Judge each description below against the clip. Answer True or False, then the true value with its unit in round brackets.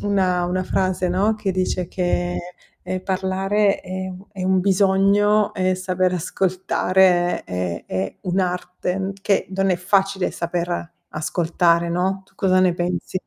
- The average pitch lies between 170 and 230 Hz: True (185 Hz)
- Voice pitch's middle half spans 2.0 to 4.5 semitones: False (1.4 semitones)